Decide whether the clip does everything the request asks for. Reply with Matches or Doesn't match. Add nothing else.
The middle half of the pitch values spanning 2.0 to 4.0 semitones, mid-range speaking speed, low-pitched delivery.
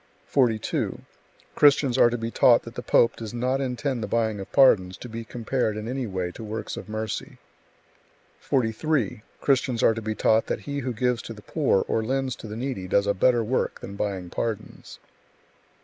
Matches